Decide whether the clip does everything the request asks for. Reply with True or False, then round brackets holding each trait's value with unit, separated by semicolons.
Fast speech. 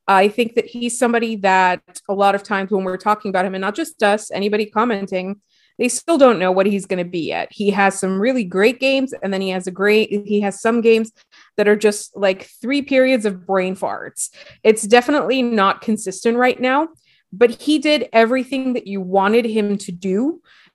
True (210 wpm)